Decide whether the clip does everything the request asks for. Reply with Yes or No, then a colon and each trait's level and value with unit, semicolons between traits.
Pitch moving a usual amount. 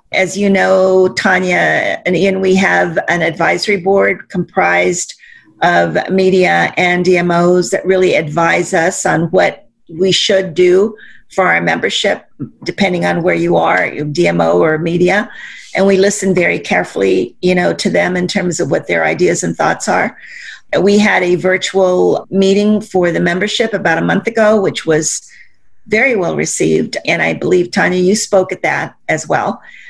No: narrow, 2.1 semitones